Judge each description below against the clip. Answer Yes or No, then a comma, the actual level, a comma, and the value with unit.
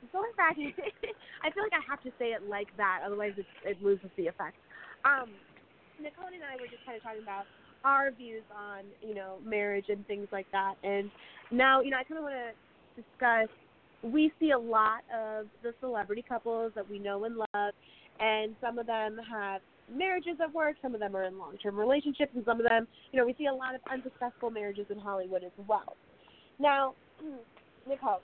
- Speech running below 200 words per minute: No, fast, 205 wpm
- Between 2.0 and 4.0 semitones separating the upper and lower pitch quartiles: No, average, 4.7 semitones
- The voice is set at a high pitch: Yes, high, 230 Hz